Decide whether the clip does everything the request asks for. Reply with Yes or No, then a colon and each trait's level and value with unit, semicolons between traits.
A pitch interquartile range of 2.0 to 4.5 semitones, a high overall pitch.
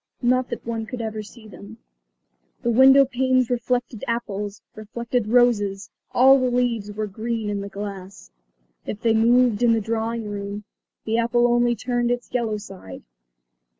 Yes: average, 2.7 semitones; high, 230 Hz